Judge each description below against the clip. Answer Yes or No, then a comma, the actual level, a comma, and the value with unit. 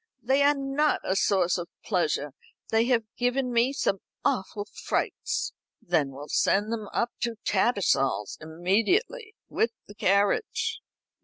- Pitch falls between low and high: No, high, 215 Hz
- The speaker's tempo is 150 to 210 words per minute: No, slow, 135 wpm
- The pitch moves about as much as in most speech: No, wide, 6.6 semitones